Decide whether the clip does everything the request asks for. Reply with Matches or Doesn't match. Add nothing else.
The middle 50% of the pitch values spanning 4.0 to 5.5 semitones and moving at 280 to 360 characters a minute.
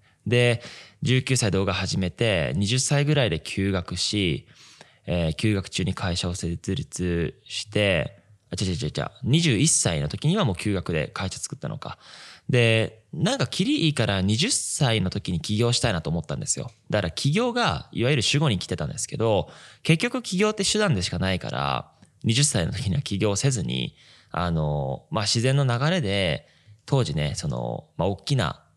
Doesn't match